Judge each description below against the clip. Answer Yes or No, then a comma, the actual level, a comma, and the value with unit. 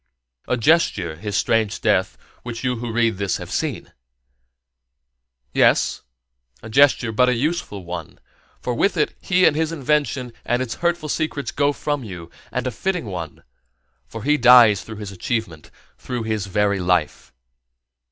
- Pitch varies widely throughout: Yes, wide, 6.0 semitones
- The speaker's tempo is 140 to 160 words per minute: Yes, average, 150 wpm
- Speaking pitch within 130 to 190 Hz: No, low, 120 Hz